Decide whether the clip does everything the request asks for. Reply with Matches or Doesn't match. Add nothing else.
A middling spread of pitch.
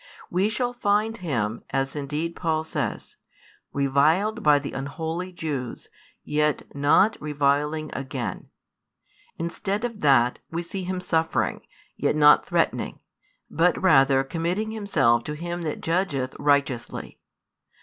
Matches